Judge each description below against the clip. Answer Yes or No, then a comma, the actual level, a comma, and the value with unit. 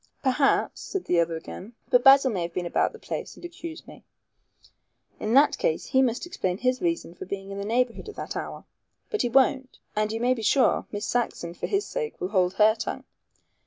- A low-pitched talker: No, high, 245 Hz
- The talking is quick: Yes, fast, 220 wpm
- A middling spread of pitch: No, wide, 5.7 semitones